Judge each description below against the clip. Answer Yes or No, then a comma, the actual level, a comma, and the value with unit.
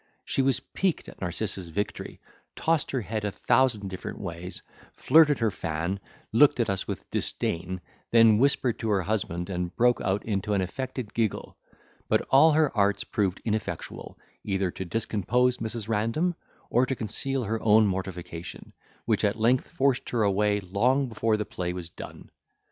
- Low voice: Yes, low, 110 Hz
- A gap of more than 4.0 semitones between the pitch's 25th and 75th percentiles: Yes, average, 4.5 semitones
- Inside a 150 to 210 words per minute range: Yes, average, 165 wpm